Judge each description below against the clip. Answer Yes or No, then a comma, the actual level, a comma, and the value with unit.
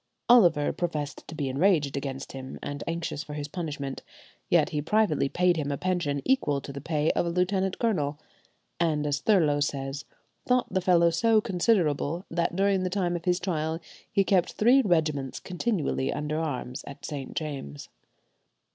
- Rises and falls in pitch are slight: No, average, 4.2 semitones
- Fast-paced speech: No, average, 170 wpm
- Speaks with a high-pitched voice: No, medium, 160 Hz